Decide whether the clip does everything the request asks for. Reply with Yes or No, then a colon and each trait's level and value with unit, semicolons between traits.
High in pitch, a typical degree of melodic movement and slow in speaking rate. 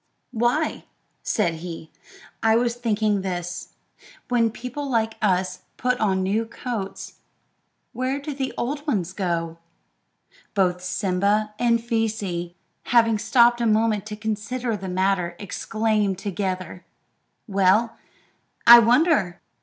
Yes: high, 215 Hz; average, 4.1 semitones; slow, 120 wpm